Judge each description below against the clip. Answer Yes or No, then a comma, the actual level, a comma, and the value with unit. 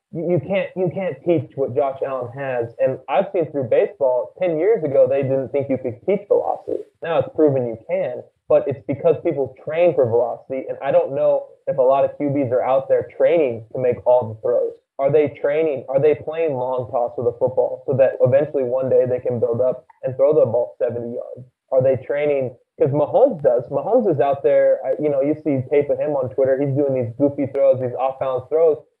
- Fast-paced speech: Yes, fast, 225 wpm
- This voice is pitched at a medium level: Yes, medium, 165 Hz